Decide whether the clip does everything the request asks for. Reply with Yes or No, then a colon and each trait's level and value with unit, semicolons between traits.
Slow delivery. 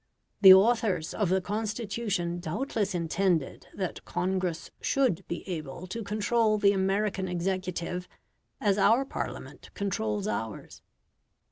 Yes: slow, 115 wpm